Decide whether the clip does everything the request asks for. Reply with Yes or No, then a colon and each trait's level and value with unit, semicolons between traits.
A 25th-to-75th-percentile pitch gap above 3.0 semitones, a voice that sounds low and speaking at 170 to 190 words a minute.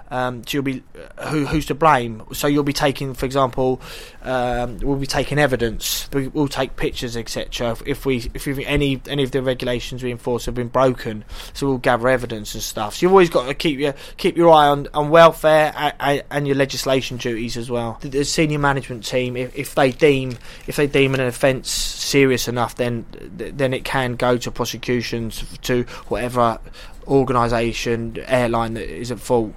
No: average, 2.7 semitones; low, 130 Hz; average, 185 wpm